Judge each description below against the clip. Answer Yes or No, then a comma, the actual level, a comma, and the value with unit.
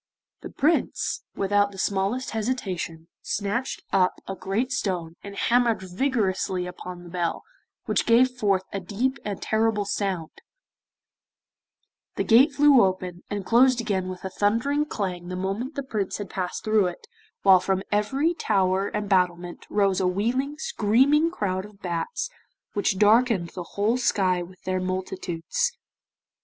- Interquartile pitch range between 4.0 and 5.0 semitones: Yes, average, 4.5 semitones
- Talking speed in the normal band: Yes, average, 150 wpm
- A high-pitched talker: Yes, high, 200 Hz